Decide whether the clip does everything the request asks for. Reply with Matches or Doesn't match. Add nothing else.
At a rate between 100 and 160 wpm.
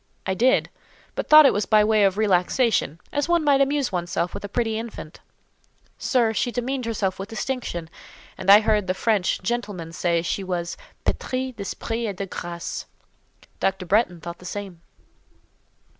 Doesn't match